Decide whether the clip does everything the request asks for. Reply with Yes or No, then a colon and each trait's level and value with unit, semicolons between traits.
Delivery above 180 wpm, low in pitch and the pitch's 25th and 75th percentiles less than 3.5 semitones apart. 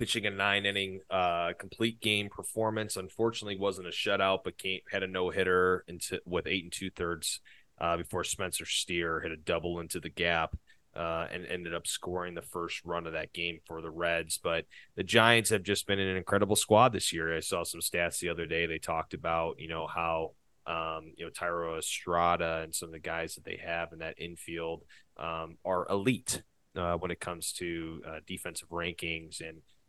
Yes: average, 195 wpm; very low, 85 Hz; average, 2.8 semitones